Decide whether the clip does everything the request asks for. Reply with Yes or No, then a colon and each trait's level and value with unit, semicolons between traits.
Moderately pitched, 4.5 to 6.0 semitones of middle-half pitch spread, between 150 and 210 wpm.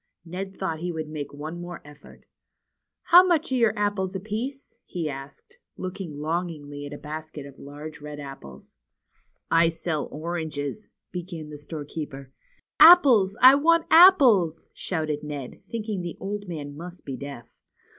Yes: medium, 165 Hz; average, 5.3 semitones; average, 160 wpm